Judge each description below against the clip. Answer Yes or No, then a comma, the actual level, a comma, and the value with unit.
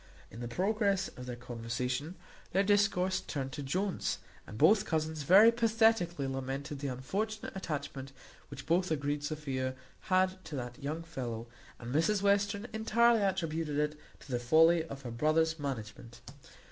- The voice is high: No, medium, 155 Hz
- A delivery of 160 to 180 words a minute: No, average, 150 wpm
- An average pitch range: No, wide, 6.3 semitones